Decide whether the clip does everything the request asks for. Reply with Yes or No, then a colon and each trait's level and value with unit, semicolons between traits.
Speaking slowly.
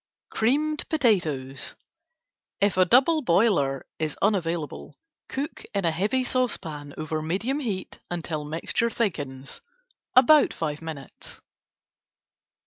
Yes: slow, 105 wpm